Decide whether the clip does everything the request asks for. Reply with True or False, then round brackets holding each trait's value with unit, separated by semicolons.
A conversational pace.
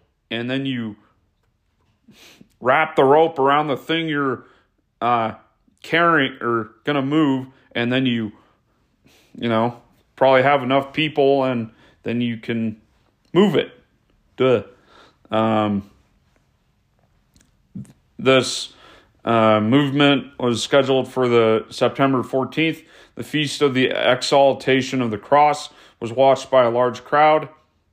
False (120 wpm)